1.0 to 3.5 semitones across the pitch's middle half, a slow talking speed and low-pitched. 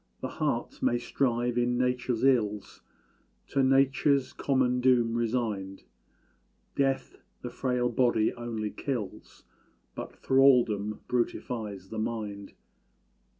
Yes: average, 2.9 semitones; slow, 105 wpm; low, 120 Hz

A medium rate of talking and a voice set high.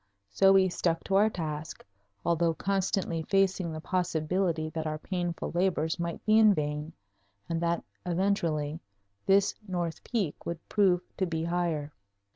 No: average, 145 wpm; medium, 170 Hz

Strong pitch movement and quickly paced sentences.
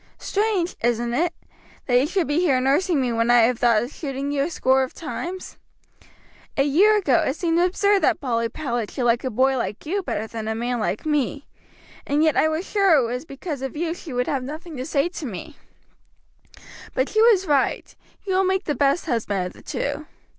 Yes: wide, 5.7 semitones; fast, 215 wpm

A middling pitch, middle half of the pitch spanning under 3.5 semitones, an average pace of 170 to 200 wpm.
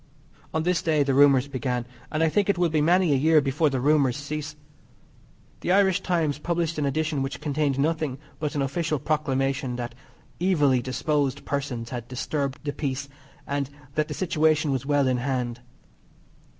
Yes: medium, 145 Hz; average, 2.8 semitones; average, 175 wpm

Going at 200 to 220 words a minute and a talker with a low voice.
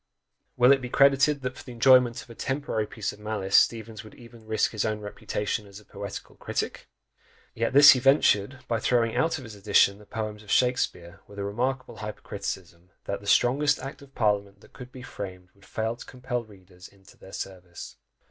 Yes: fast, 205 wpm; low, 110 Hz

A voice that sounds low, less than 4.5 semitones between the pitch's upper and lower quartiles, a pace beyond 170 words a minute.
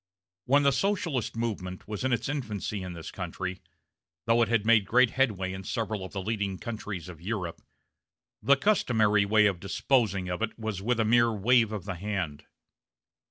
Yes: low, 105 Hz; average, 3.8 semitones; average, 180 wpm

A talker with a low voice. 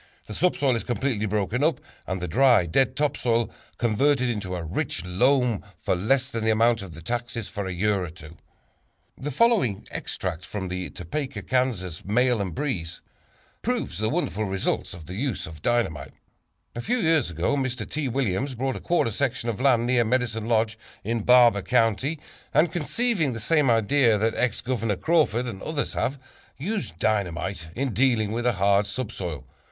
Yes: low, 115 Hz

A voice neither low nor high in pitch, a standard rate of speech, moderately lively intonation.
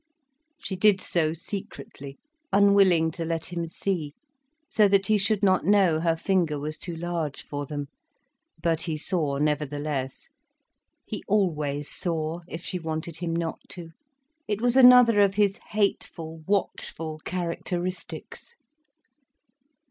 No: medium, 170 Hz; slow, 130 wpm; average, 3.9 semitones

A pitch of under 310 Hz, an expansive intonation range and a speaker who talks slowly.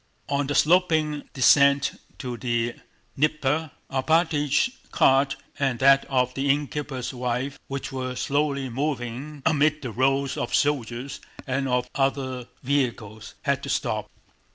No: low, 135 Hz; narrow, 2.4 semitones; slow, 130 wpm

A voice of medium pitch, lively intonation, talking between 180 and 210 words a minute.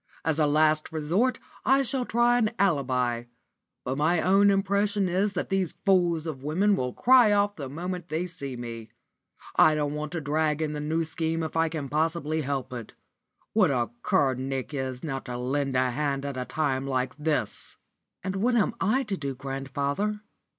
Yes: medium, 155 Hz; wide, 5.8 semitones; average, 185 wpm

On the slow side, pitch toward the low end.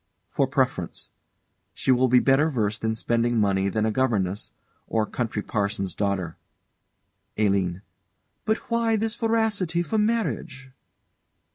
Yes: slow, 125 wpm; low, 120 Hz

